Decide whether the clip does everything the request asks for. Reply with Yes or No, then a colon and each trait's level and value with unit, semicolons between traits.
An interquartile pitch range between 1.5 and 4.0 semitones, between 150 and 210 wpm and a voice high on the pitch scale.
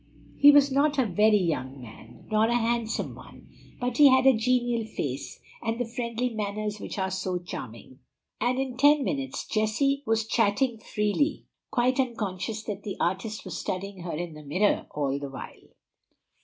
No: average, 5.1 semitones; average, 170 wpm; high, 220 Hz